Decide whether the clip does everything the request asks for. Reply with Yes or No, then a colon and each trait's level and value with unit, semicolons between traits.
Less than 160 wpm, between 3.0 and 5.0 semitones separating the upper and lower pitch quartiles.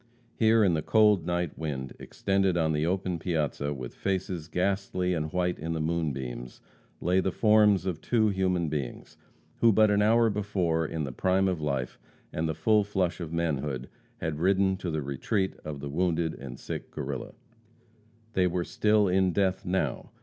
No: average, 175 wpm; average, 3.9 semitones